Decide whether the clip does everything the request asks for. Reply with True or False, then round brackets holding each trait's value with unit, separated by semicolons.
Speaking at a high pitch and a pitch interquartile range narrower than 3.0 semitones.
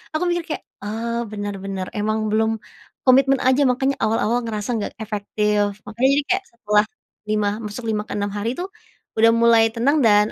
False (220 Hz; 3.4 semitones)